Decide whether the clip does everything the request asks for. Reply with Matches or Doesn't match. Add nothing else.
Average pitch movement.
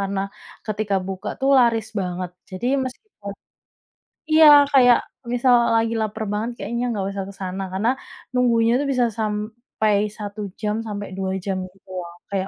Matches